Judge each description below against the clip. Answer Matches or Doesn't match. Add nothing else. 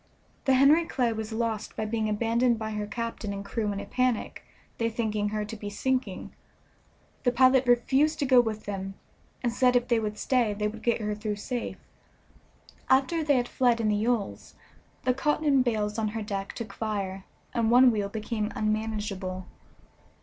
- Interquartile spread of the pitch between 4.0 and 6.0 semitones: Doesn't match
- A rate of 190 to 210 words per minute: Doesn't match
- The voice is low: Doesn't match